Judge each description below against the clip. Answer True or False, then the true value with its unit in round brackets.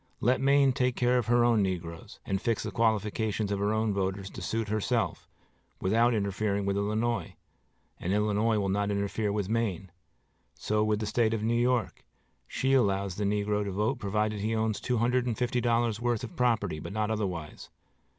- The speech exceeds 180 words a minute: True (190 wpm)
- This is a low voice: True (110 Hz)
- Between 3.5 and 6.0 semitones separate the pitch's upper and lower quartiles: False (2.7 semitones)